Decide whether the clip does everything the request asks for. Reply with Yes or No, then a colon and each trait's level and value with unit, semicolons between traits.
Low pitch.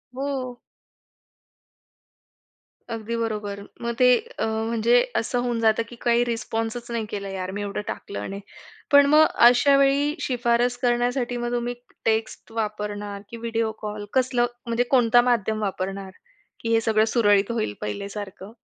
No: high, 230 Hz